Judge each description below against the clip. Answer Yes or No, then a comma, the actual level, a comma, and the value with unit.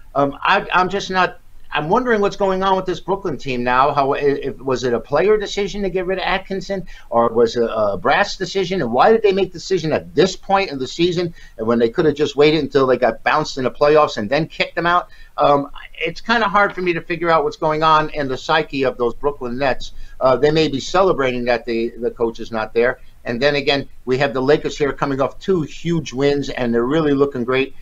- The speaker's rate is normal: No, fast, 250 wpm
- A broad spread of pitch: Yes, wide, 5.8 semitones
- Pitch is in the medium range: Yes, medium, 150 Hz